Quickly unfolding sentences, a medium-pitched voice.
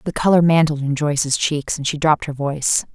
Yes: fast, 225 wpm; medium, 150 Hz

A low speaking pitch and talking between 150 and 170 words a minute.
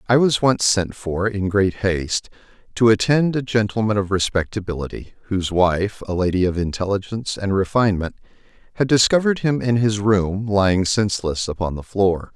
Yes: low, 100 Hz; average, 160 wpm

